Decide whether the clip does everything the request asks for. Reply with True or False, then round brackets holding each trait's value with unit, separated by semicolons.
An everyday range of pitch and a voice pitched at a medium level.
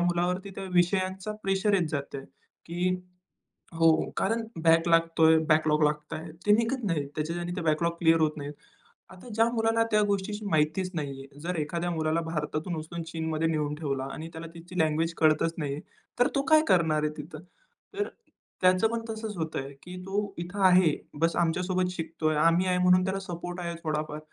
True (3.0 semitones; 170 Hz)